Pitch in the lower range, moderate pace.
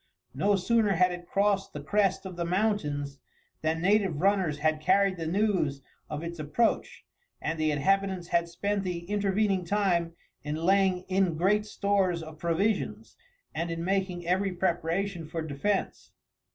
No: medium, 180 Hz; average, 150 wpm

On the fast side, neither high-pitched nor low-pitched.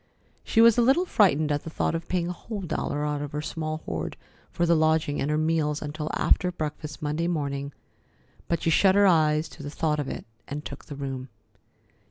Yes: fast, 215 wpm; medium, 155 Hz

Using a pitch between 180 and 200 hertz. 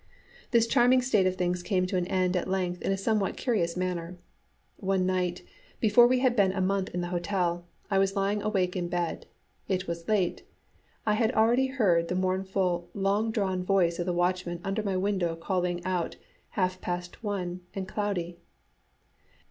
Yes: medium, 185 Hz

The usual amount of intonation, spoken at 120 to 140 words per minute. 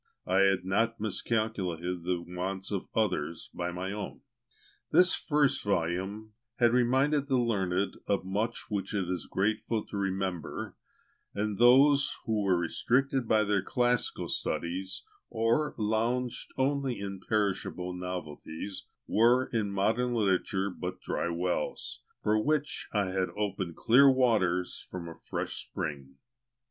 Yes: average, 4.3 semitones; slow, 135 wpm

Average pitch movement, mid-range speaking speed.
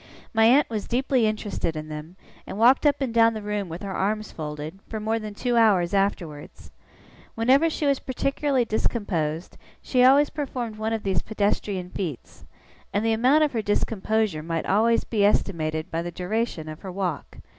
Yes: average, 4.7 semitones; average, 180 wpm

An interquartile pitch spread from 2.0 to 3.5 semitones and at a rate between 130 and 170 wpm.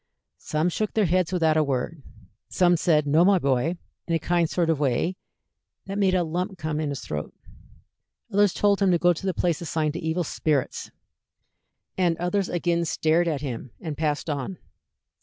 No: average, 2.8 semitones; average, 185 wpm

